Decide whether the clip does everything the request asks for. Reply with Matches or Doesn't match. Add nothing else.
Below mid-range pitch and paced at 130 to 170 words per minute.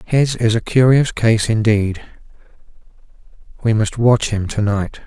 Matches